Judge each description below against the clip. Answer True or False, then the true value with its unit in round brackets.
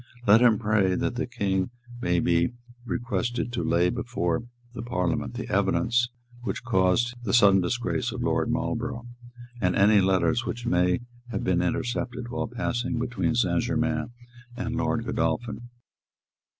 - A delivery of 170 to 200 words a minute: False (140 wpm)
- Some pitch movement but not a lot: True (4.7 semitones)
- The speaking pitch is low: True (115 Hz)